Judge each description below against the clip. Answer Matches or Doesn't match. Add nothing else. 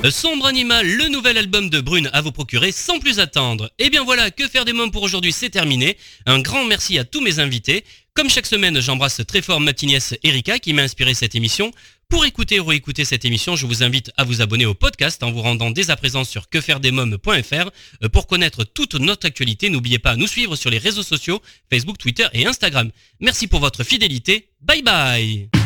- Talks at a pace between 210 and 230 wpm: Matches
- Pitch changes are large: Matches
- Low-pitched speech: Doesn't match